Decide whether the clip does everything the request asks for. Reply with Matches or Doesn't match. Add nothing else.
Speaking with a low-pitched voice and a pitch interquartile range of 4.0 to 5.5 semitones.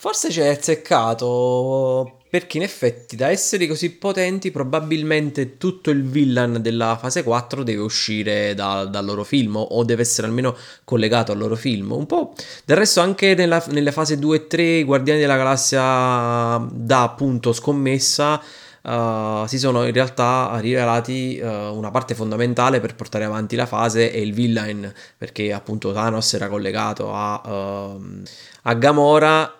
Matches